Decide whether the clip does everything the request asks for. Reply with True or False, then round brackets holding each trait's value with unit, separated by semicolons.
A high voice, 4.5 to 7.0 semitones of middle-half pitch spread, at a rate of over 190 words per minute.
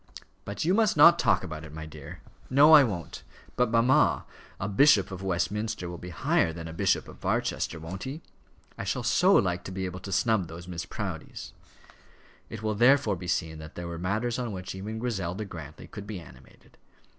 False (95 Hz; 4.9 semitones; 200 wpm)